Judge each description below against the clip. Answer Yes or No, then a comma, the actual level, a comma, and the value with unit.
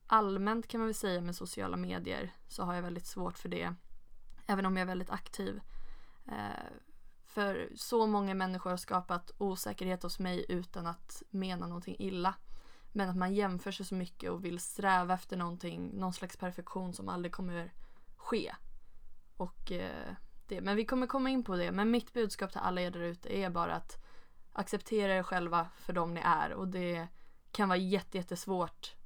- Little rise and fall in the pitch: Yes, narrow, 2.2 semitones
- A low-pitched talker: No, medium, 185 Hz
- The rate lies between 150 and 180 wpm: Yes, average, 175 wpm